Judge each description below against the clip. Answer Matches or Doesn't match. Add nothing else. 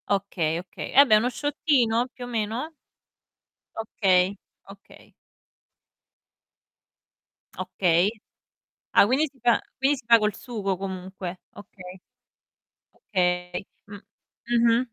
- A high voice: Matches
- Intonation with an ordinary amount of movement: Matches